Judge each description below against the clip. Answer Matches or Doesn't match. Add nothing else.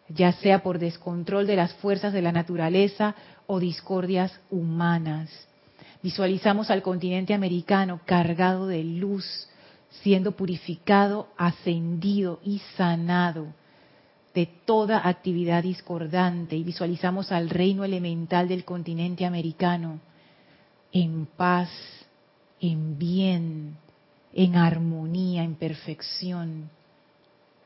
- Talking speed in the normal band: Doesn't match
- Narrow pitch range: Matches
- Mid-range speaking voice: Matches